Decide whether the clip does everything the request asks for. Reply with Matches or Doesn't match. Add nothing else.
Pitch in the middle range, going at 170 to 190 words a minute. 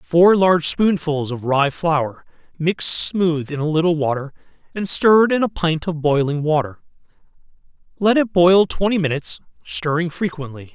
Doesn't match